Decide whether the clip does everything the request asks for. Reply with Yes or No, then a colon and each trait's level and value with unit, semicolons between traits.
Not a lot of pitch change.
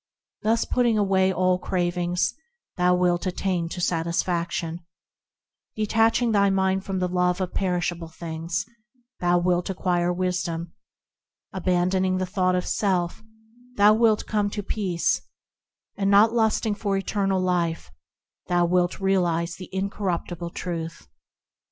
Yes: narrow, 2.0 semitones